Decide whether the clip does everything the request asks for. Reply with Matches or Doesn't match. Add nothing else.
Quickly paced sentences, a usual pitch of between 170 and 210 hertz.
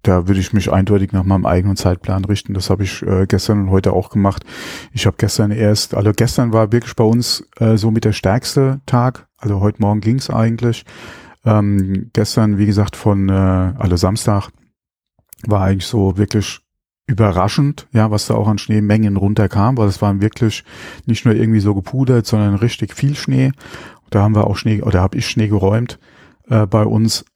Doesn't match